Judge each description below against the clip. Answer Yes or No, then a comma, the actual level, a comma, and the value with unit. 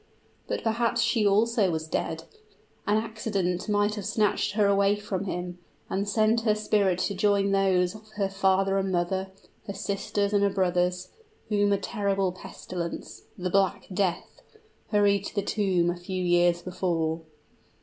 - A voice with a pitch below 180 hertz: No, high, 195 Hz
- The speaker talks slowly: No, average, 160 wpm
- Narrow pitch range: Yes, narrow, 2.3 semitones